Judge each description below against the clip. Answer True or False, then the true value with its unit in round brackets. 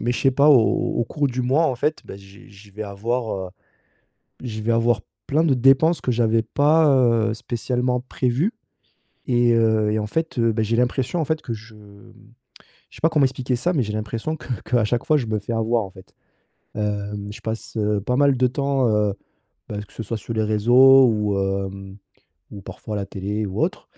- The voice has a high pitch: False (115 Hz)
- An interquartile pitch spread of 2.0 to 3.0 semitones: False (3.6 semitones)